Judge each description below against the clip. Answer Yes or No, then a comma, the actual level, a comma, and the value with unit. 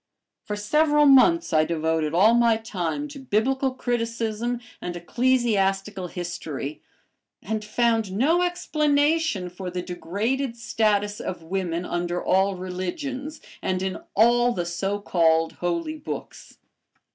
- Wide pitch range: Yes, wide, 6.1 semitones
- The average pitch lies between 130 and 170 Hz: No, high, 210 Hz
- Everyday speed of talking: No, slow, 120 wpm